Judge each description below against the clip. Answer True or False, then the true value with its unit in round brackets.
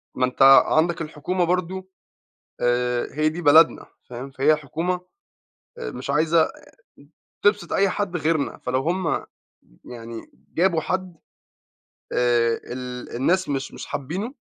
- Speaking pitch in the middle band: True (155 Hz)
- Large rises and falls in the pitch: True (5.9 semitones)